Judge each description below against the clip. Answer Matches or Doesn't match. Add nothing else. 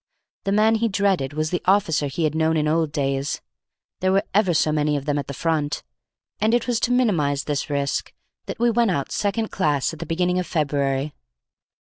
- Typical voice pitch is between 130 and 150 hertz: Doesn't match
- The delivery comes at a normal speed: Doesn't match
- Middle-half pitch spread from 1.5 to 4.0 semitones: Doesn't match